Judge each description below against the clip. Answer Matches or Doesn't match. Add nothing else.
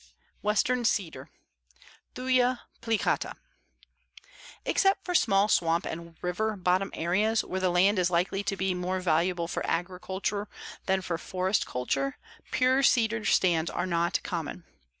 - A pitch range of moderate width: Matches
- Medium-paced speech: Doesn't match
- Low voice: Doesn't match